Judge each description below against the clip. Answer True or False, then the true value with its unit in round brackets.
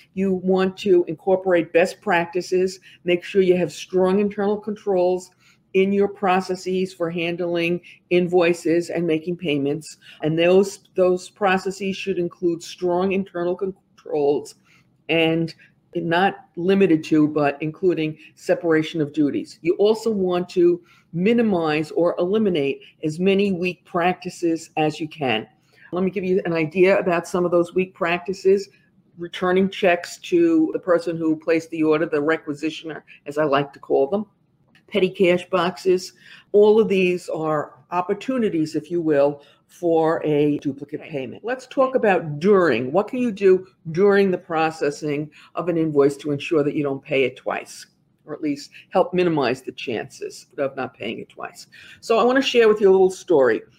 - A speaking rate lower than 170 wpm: True (160 wpm)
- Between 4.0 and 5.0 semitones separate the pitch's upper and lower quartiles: False (3.1 semitones)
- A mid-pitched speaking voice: True (175 Hz)